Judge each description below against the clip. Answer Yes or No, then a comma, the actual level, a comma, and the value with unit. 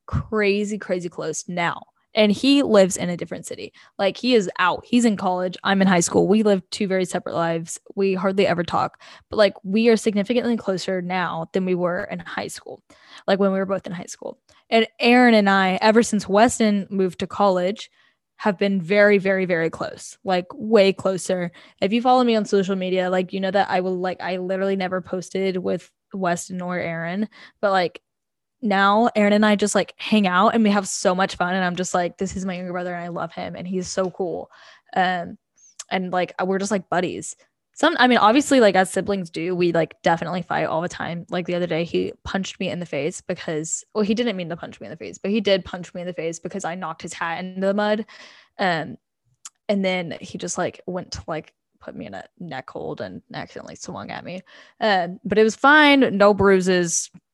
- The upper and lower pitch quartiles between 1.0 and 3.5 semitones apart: Yes, narrow, 2.5 semitones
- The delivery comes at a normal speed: No, fast, 225 wpm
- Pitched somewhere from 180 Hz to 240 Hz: Yes, high, 190 Hz